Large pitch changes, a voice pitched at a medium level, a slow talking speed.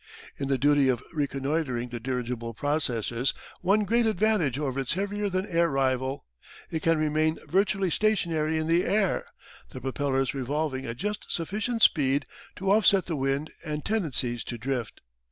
No: wide, 5.9 semitones; medium, 150 Hz; average, 160 wpm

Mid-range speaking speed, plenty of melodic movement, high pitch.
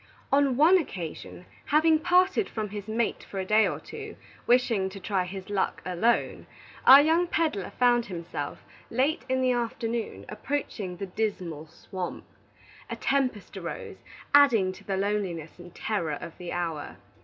Yes: average, 155 wpm; wide, 6.1 semitones; high, 210 Hz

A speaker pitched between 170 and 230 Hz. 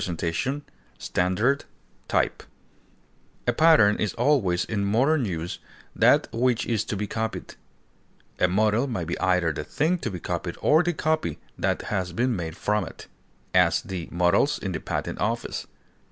No: low, 105 Hz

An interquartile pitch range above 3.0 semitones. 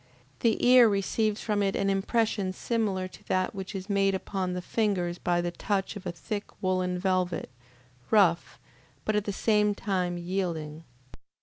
No: narrow, 2.5 semitones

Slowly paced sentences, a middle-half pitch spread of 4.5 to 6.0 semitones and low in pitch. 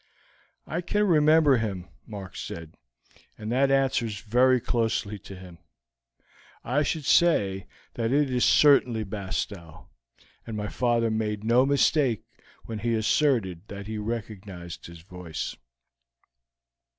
Yes: slow, 125 wpm; average, 4.9 semitones; low, 110 Hz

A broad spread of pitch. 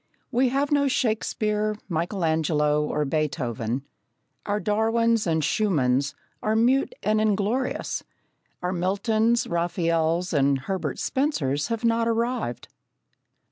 Yes: wide, 7.0 semitones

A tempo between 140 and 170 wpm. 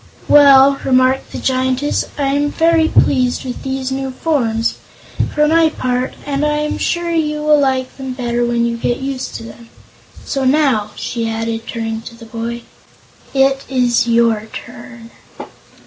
Yes: average, 155 wpm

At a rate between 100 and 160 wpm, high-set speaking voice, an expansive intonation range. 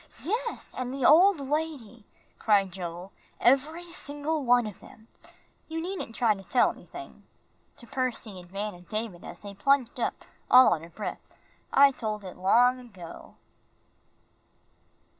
Yes: average, 150 wpm; high, 240 Hz; wide, 6.0 semitones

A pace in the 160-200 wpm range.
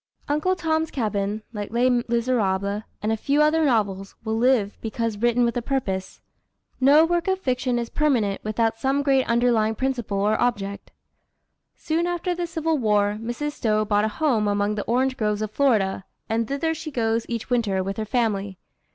Yes: average, 175 wpm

